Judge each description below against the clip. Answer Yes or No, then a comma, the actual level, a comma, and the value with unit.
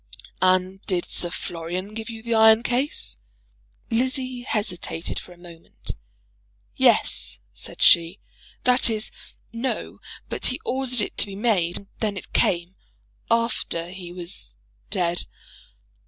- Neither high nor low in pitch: No, high, 200 Hz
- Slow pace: Yes, slow, 130 wpm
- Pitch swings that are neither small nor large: Yes, average, 4.9 semitones